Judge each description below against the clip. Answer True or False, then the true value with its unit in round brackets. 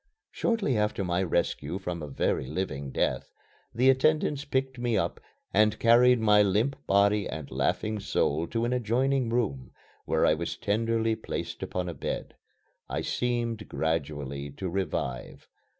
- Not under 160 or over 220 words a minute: False (150 wpm)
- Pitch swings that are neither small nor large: False (6.1 semitones)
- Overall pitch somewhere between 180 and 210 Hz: False (105 Hz)